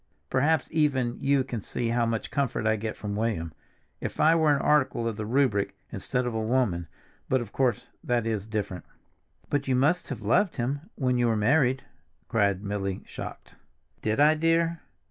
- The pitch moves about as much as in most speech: Yes, average, 4.5 semitones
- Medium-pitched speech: No, low, 120 Hz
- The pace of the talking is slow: No, average, 180 wpm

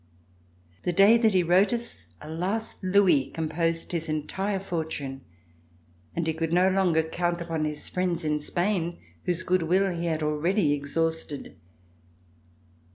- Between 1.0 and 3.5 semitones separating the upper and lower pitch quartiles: Yes, average, 2.8 semitones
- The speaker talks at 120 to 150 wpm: Yes, average, 145 wpm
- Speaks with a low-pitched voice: No, medium, 170 Hz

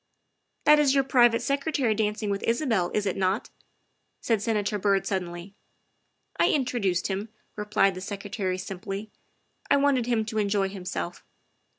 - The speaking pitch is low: No, high, 210 Hz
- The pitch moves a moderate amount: Yes, average, 3.7 semitones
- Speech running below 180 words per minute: Yes, average, 170 wpm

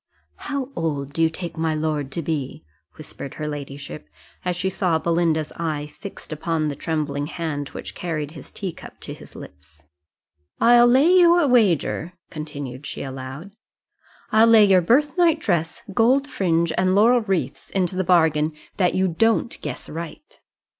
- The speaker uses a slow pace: No, average, 160 wpm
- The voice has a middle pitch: Yes, medium, 165 Hz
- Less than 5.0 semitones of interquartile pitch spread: No, average, 5.3 semitones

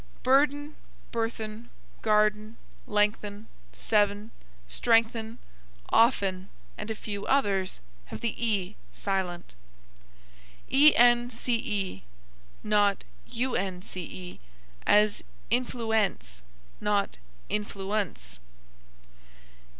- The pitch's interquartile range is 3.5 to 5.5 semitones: No, average, 2.8 semitones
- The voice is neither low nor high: No, high, 210 Hz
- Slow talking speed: Yes, slow, 70 wpm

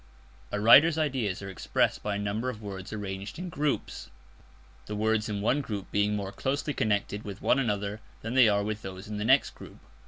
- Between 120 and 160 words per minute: No, fast, 205 wpm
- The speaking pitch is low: Yes, low, 105 Hz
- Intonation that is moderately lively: Yes, average, 3.8 semitones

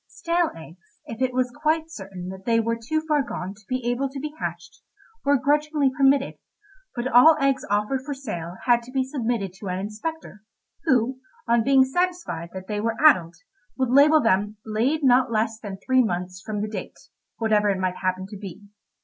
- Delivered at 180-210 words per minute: Yes, average, 190 wpm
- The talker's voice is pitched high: Yes, high, 235 Hz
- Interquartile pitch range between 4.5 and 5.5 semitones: Yes, average, 5.2 semitones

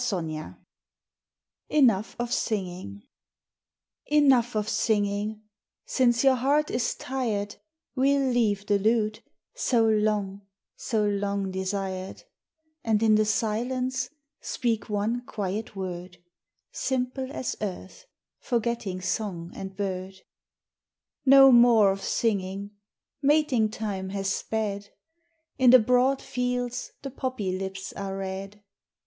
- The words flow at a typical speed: No, slow, 110 wpm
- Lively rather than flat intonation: No, average, 4.1 semitones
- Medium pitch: No, high, 215 Hz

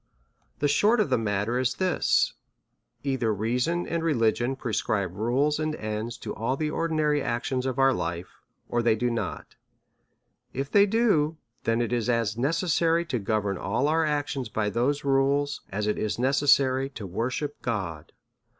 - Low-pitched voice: Yes, low, 130 Hz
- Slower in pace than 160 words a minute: No, average, 165 wpm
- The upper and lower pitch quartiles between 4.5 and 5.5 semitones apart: Yes, average, 4.9 semitones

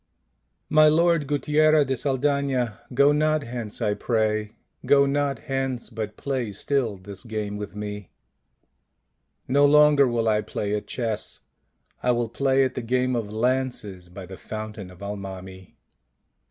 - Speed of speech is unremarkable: Yes, average, 155 wpm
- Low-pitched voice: Yes, low, 120 Hz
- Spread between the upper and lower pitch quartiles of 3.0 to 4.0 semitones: No, average, 5.1 semitones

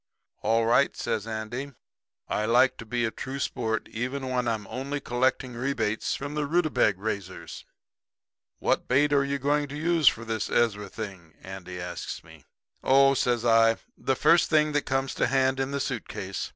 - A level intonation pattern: No, average, 3.9 semitones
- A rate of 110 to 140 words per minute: No, average, 180 wpm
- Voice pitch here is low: Yes, low, 125 Hz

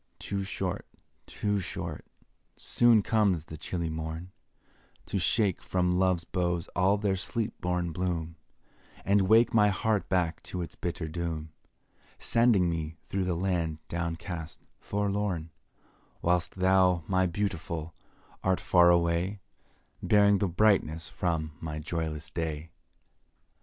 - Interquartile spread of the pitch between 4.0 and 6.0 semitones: No, average, 2.9 semitones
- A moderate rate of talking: No, slow, 125 wpm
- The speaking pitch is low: Yes, very low, 90 Hz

